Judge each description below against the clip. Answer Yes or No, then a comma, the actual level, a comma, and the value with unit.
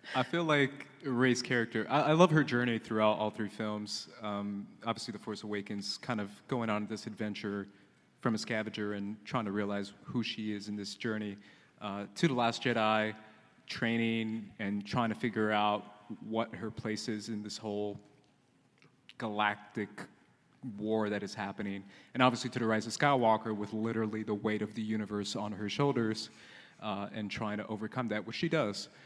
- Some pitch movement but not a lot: No, narrow, 1.8 semitones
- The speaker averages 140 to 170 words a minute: No, average, 180 wpm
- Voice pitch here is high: No, low, 110 Hz